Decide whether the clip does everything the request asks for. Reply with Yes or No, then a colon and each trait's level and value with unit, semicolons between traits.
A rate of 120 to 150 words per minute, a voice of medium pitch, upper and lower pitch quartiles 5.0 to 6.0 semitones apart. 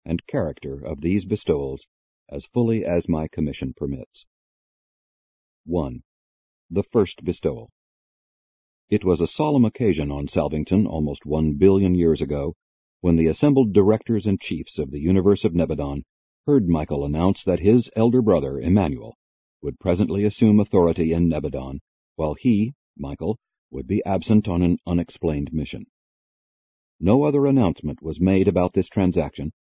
No: average, 140 wpm; very low, 85 Hz; wide, 5.4 semitones